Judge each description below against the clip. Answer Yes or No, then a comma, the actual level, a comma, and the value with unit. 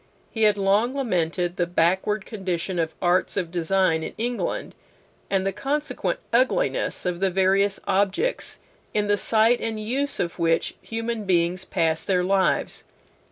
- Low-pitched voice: No, high, 195 Hz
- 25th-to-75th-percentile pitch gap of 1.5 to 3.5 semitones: No, average, 3.9 semitones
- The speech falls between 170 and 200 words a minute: No, average, 150 wpm